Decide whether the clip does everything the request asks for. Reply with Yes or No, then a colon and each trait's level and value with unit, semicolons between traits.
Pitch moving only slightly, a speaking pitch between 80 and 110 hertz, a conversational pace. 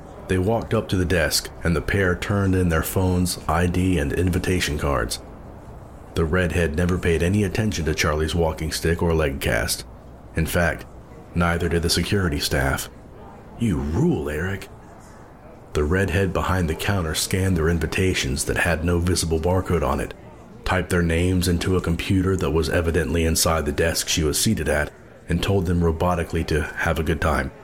Yes: narrow, 2.3 semitones; very low, 85 Hz; average, 175 wpm